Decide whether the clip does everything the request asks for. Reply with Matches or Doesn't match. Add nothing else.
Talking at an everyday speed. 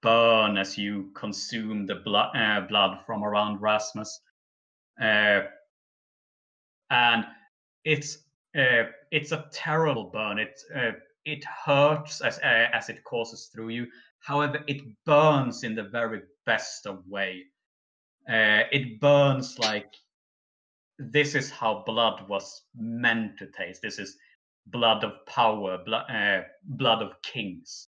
Doesn't match